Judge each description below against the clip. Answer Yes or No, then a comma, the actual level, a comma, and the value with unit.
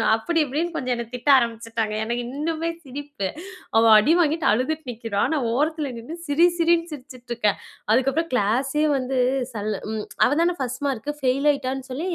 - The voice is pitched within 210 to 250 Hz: No, very high, 265 Hz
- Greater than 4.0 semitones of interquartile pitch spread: Yes, average, 4.5 semitones